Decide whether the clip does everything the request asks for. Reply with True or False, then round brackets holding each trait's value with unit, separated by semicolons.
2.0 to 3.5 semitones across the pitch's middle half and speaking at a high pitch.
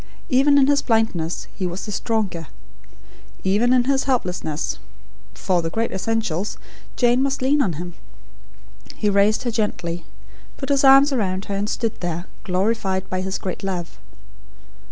False (5.4 semitones; 205 Hz)